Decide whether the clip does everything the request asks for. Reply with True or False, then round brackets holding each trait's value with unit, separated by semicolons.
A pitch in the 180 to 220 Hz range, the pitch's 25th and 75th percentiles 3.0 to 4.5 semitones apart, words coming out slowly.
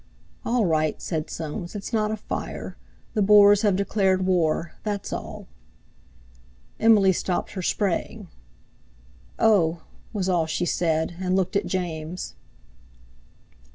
True (185 Hz; 3.4 semitones; 120 wpm)